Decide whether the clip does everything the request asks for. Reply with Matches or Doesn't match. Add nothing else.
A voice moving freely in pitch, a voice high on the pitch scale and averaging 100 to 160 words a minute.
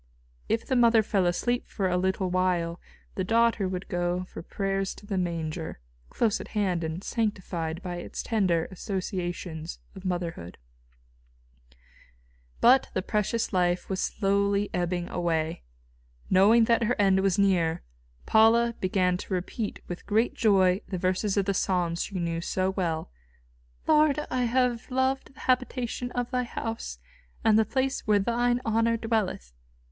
Doesn't match